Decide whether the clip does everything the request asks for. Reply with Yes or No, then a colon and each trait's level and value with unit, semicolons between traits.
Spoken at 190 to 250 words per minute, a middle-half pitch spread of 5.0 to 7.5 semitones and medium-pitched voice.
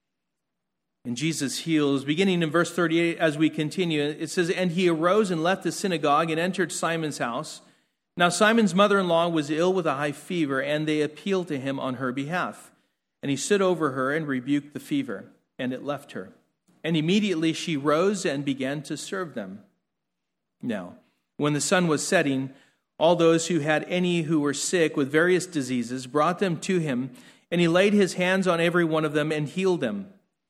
No: average, 195 wpm; average, 3.7 semitones; medium, 160 Hz